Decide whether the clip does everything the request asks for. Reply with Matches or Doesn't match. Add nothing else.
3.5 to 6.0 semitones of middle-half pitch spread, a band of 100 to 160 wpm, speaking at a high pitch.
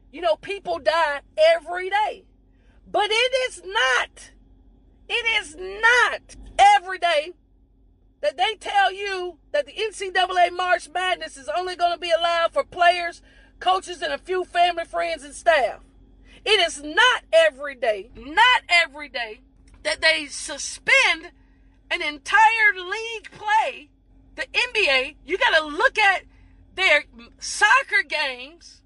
Matches